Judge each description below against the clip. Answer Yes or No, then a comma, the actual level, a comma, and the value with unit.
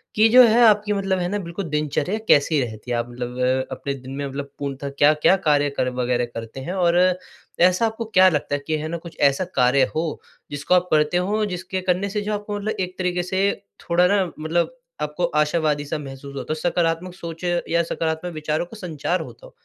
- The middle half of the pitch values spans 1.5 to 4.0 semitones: No, average, 4.5 semitones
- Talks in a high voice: No, medium, 165 Hz